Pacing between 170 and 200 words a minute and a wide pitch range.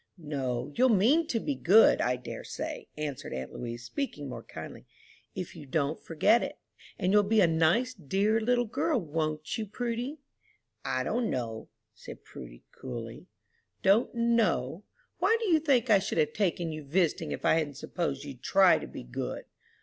Yes: average, 175 wpm; wide, 8.4 semitones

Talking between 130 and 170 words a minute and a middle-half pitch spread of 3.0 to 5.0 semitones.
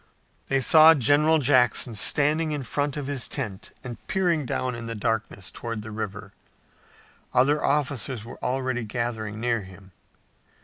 Yes: average, 145 wpm; average, 4.6 semitones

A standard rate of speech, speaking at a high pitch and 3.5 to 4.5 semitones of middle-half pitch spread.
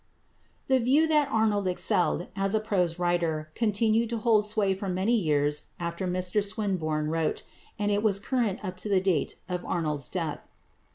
Yes: average, 170 wpm; high, 195 Hz; average, 3.9 semitones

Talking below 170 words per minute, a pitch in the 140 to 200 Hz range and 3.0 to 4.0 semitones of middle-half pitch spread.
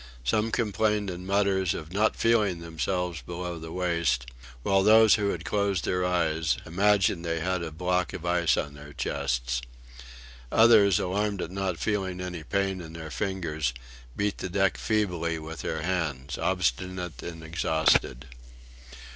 No: average, 150 wpm; very low, 90 Hz; average, 3.4 semitones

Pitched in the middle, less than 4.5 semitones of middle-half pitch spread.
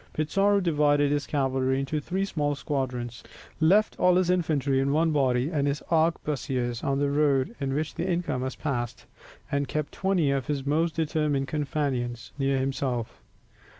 Yes: medium, 145 Hz; average, 2.9 semitones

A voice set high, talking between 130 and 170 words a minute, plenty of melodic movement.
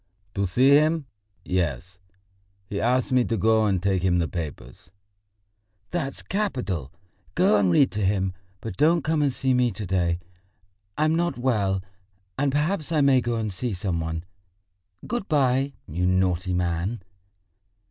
No: low, 110 Hz; average, 155 wpm; wide, 7.1 semitones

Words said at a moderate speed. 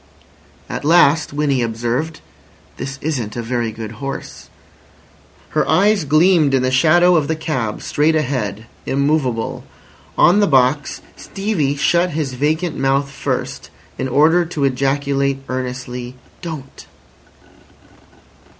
No: slow, 120 wpm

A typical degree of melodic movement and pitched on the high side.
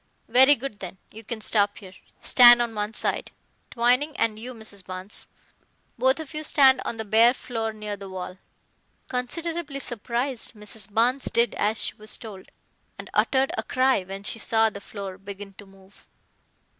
Yes: average, 3.8 semitones; high, 225 Hz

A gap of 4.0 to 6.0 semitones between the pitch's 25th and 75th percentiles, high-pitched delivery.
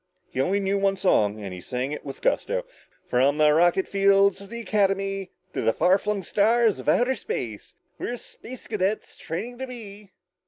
Yes: average, 5.1 semitones; high, 195 Hz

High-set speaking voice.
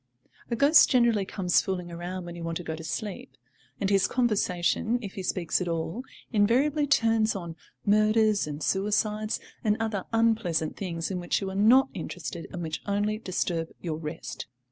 Yes: high, 195 Hz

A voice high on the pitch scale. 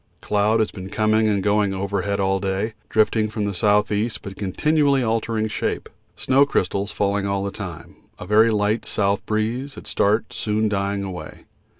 No: low, 105 Hz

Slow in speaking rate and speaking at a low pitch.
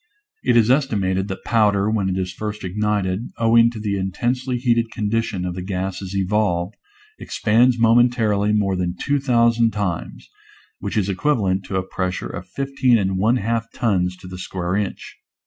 No: average, 170 wpm; low, 105 Hz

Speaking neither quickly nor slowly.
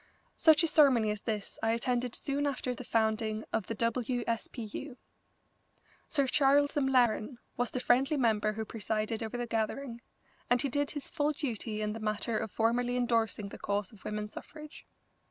Yes: average, 180 wpm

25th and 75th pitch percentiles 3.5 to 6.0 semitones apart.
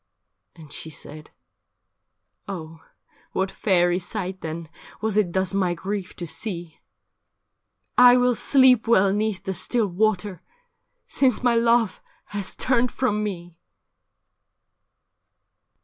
Yes: average, 4.4 semitones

